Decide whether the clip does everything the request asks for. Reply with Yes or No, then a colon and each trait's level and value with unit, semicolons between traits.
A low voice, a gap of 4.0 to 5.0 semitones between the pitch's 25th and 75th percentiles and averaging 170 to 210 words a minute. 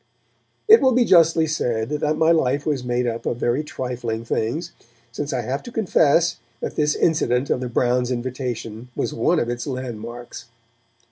Yes: low, 125 Hz; average, 4.3 semitones; average, 175 wpm